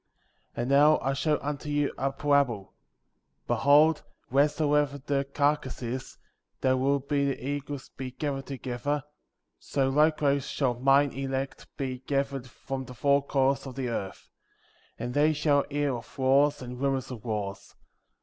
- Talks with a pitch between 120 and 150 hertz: Yes, medium, 140 Hz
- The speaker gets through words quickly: No, average, 155 wpm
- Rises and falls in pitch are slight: Yes, narrow, 1.8 semitones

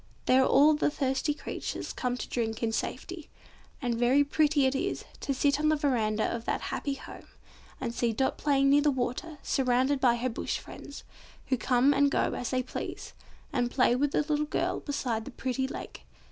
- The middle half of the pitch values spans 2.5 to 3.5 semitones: Yes, average, 2.8 semitones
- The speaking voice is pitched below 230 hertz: No, very high, 265 Hz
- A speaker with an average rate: Yes, average, 195 wpm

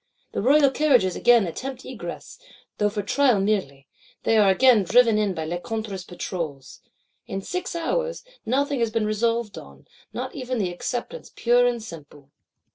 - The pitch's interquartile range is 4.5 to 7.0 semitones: Yes, average, 5.2 semitones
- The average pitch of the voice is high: Yes, high, 220 Hz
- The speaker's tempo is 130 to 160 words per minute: Yes, average, 150 wpm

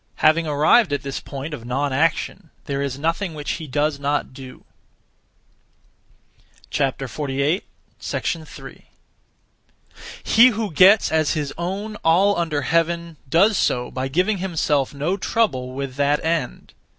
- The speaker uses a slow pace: Yes, slow, 125 wpm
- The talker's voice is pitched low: No, medium, 155 Hz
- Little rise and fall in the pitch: No, average, 3.8 semitones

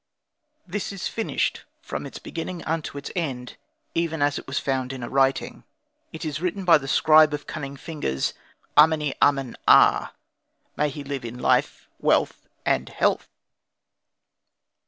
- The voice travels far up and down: No, average, 3.1 semitones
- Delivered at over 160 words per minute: No, average, 150 wpm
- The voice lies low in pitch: No, medium, 145 Hz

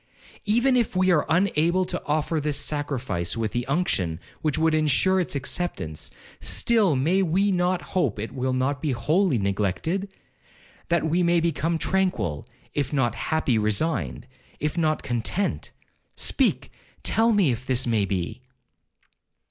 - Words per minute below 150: Yes, average, 140 wpm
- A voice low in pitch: No, medium, 155 Hz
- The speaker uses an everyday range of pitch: No, wide, 6.8 semitones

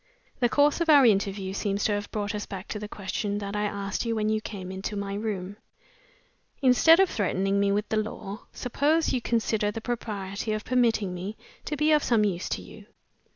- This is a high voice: Yes, high, 210 Hz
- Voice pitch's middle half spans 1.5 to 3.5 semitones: Yes, average, 2.8 semitones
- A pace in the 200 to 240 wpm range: Yes, fast, 205 wpm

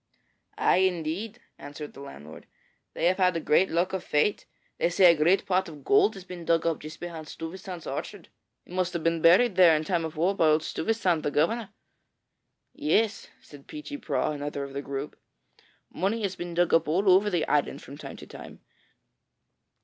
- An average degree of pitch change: Yes, average, 3.6 semitones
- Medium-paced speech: Yes, average, 190 wpm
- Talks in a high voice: No, medium, 170 Hz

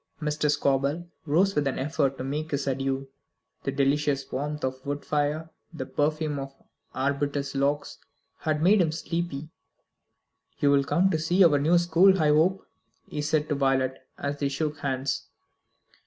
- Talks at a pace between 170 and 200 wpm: No, average, 160 wpm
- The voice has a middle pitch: Yes, medium, 145 Hz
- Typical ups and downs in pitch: No, narrow, 2.2 semitones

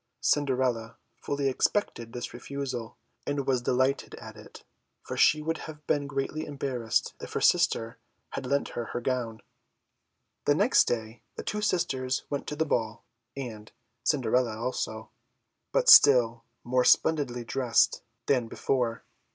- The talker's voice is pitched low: Yes, low, 130 Hz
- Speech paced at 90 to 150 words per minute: Yes, average, 140 wpm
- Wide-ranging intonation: No, average, 3.3 semitones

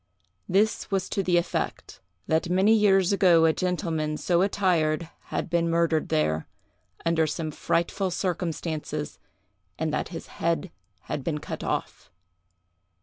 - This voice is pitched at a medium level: Yes, medium, 170 Hz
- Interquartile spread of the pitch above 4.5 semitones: No, average, 2.7 semitones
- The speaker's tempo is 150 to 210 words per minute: No, slow, 135 wpm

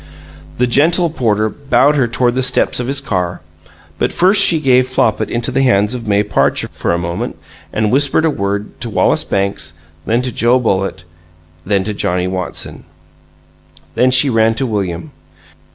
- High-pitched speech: No, low, 120 Hz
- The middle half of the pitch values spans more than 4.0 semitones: Yes, average, 4.7 semitones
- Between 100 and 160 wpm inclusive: No, average, 170 wpm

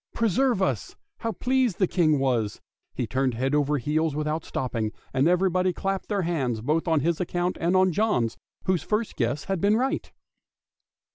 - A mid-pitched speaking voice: Yes, medium, 165 Hz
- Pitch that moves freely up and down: Yes, wide, 6.0 semitones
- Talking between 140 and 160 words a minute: No, average, 180 wpm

